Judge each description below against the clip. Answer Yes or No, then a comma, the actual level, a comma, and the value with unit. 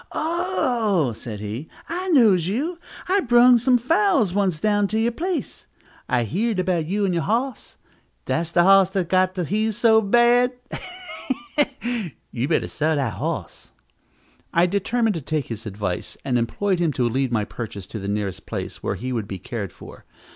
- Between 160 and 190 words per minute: Yes, average, 180 wpm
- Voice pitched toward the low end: No, high, 190 Hz